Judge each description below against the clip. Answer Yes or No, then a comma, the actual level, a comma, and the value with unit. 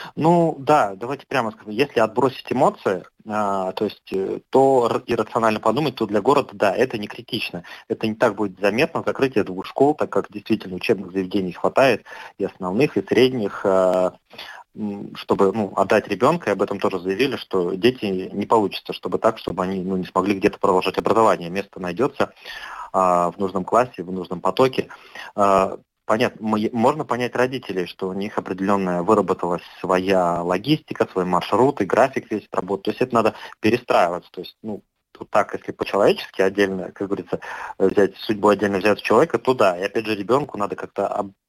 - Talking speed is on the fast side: Yes, fast, 165 wpm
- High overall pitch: No, low, 100 Hz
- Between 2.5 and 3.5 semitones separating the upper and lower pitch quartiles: Yes, average, 2.9 semitones